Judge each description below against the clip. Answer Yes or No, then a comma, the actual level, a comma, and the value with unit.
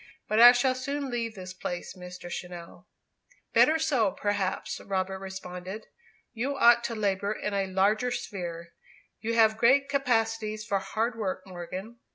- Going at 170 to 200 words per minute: No, average, 150 wpm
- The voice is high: Yes, high, 210 Hz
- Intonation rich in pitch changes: No, average, 4.1 semitones